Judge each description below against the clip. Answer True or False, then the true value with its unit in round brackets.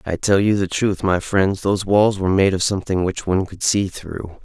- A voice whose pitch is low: True (95 Hz)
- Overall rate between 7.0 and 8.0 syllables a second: False (5.5 syllables/s)